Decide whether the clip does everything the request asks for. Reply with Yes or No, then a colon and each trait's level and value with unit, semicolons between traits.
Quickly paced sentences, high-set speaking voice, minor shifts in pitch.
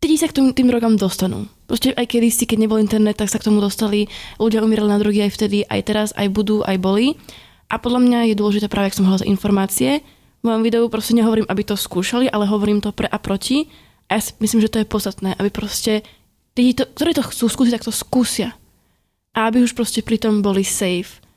Yes: fast, 220 wpm; high, 215 Hz; narrow, 2.2 semitones